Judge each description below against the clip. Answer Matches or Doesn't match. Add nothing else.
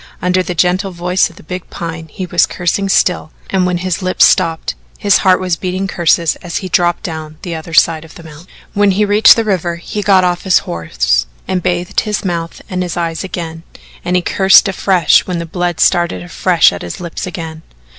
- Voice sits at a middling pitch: Matches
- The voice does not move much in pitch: Matches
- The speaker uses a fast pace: Matches